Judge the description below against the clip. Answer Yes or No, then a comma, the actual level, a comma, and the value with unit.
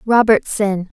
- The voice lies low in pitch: No, high, 210 Hz